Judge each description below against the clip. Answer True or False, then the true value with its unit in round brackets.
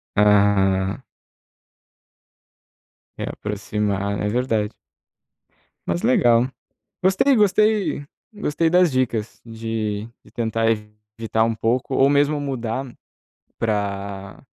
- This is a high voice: False (115 Hz)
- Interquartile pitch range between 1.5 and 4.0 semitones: False (4.7 semitones)